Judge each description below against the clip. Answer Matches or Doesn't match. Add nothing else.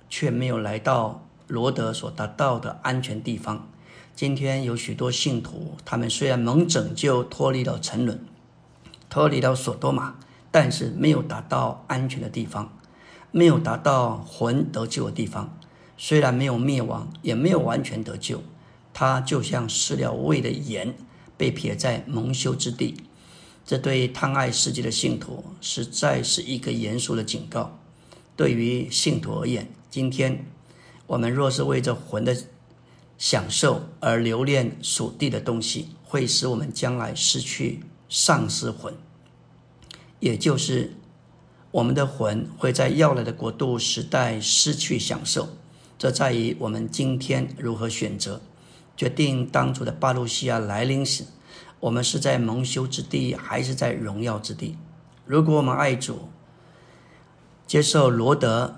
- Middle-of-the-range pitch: Doesn't match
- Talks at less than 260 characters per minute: Matches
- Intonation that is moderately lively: Matches